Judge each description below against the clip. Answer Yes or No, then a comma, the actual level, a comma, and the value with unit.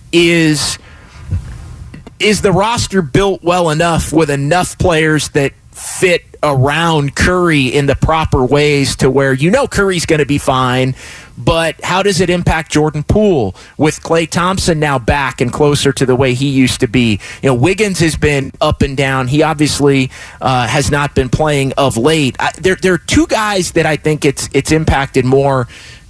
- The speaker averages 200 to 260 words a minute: No, average, 180 wpm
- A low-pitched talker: No, medium, 145 Hz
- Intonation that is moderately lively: Yes, average, 3.8 semitones